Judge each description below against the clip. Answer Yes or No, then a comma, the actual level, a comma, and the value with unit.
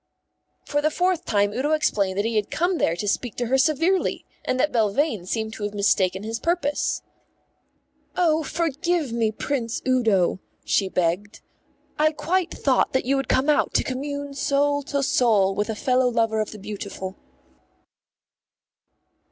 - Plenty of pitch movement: Yes, wide, 6.0 semitones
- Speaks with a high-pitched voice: Yes, very high, 250 Hz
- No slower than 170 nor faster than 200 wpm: No, average, 160 wpm